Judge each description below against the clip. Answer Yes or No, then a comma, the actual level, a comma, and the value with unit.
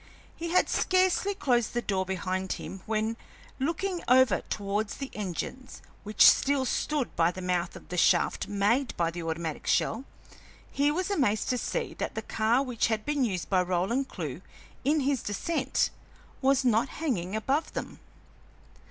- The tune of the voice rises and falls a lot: Yes, wide, 6.5 semitones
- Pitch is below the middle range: No, high, 235 Hz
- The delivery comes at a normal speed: Yes, average, 160 wpm